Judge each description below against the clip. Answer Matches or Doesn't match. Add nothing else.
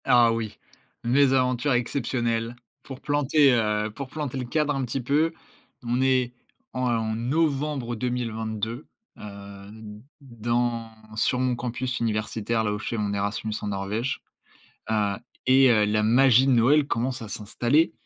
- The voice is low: Matches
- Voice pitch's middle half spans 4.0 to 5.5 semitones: Doesn't match